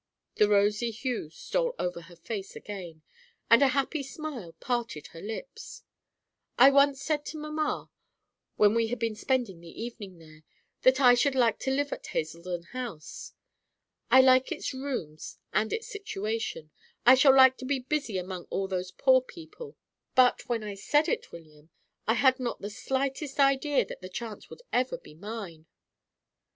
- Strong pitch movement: Yes, wide, 6.1 semitones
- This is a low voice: No, high, 235 Hz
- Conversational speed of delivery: Yes, average, 170 wpm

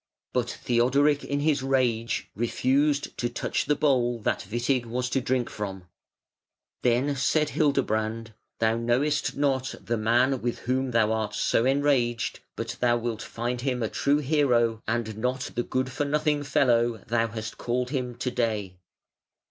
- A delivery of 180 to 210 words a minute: No, average, 155 wpm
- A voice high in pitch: No, low, 125 Hz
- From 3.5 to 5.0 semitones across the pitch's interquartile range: No, average, 2.9 semitones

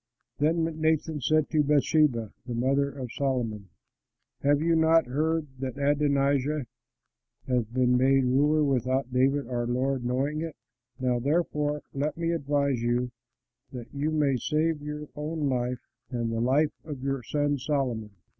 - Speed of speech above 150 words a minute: No, average, 145 wpm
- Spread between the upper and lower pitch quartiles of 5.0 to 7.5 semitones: No, average, 3.0 semitones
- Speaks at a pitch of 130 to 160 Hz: Yes, medium, 140 Hz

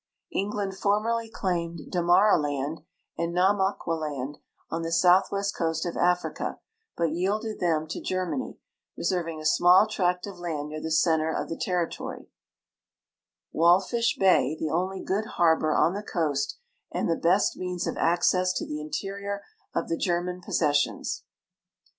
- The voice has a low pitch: No, medium, 175 Hz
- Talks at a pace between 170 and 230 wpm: No, average, 140 wpm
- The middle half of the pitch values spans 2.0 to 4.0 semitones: Yes, average, 3.1 semitones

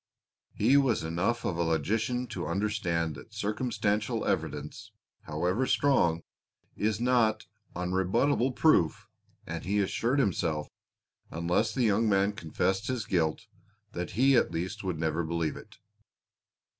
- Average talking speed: No, slow, 130 wpm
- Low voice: Yes, low, 100 Hz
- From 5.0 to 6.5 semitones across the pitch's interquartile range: Yes, wide, 5.6 semitones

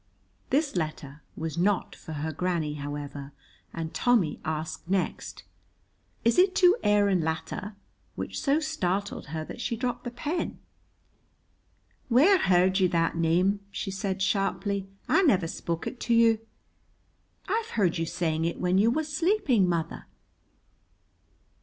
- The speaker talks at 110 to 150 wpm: Yes, average, 140 wpm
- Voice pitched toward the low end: No, high, 190 Hz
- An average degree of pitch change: No, wide, 6.5 semitones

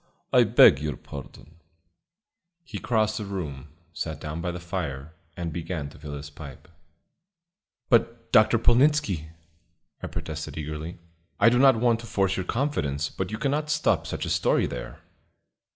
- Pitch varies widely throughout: Yes, wide, 7.2 semitones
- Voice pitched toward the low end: Yes, very low, 90 Hz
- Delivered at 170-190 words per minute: No, average, 155 wpm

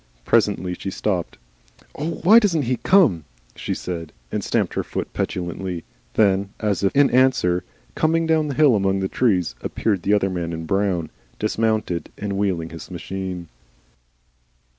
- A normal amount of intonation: No, wide, 6.0 semitones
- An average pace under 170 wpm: Yes, average, 155 wpm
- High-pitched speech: No, very low, 95 Hz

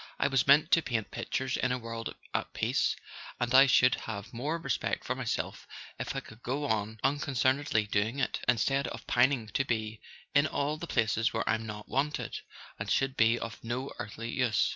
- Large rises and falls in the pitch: No, average, 3.5 semitones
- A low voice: Yes, low, 125 Hz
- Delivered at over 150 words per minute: Yes, average, 190 wpm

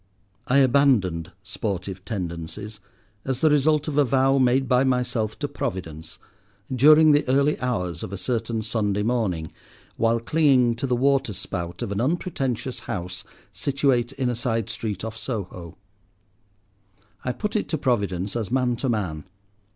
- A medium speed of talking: Yes, average, 150 wpm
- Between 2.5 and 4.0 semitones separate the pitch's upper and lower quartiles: No, average, 5.1 semitones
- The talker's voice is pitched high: No, low, 120 Hz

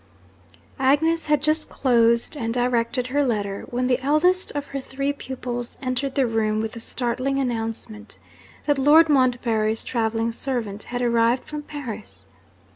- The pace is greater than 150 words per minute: No, average, 145 wpm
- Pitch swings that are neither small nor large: Yes, average, 3.4 semitones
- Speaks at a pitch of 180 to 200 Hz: No, very high, 250 Hz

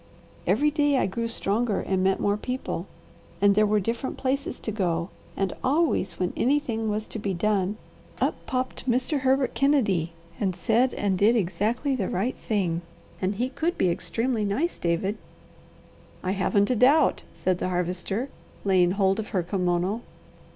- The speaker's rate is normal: Yes, average, 165 wpm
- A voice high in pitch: Yes, high, 210 Hz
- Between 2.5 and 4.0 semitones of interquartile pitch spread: No, average, 5.2 semitones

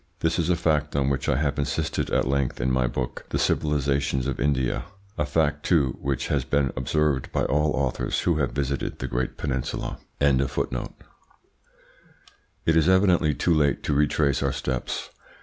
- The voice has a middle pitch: No, very low, 70 Hz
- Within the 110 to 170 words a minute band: Yes, average, 165 wpm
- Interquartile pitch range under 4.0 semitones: Yes, narrow, 2.4 semitones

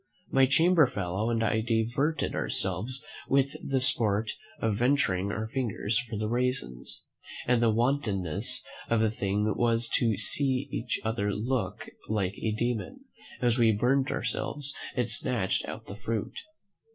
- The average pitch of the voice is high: No, low, 115 Hz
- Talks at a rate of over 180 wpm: No, average, 145 wpm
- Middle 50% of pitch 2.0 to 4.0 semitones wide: Yes, average, 3.3 semitones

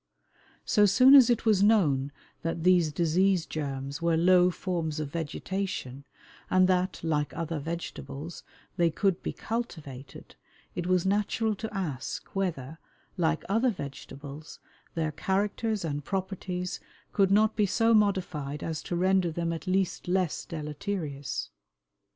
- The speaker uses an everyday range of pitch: Yes, average, 4.1 semitones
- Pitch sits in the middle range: Yes, medium, 175 Hz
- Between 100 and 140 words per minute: Yes, slow, 135 wpm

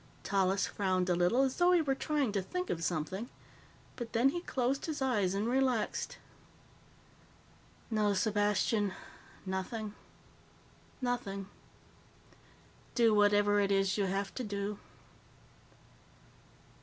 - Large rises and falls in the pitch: No, average, 4.4 semitones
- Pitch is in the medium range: No, high, 205 Hz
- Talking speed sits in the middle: No, slow, 115 wpm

